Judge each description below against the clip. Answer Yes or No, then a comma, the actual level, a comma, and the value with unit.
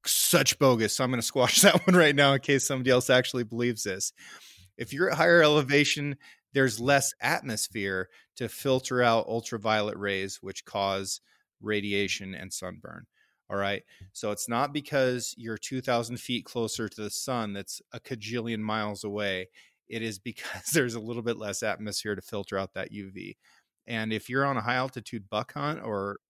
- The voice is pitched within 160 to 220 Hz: No, low, 115 Hz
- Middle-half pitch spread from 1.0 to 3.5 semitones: No, average, 4.0 semitones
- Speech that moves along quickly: No, average, 180 wpm